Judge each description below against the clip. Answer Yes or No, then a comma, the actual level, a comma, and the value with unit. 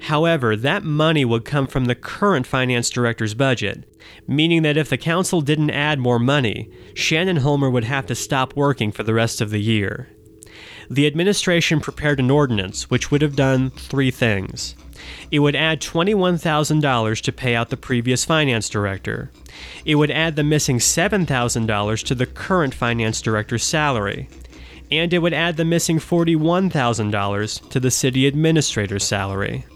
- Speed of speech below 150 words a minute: No, average, 155 wpm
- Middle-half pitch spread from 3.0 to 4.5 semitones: No, wide, 5.5 semitones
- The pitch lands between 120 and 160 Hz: Yes, low, 135 Hz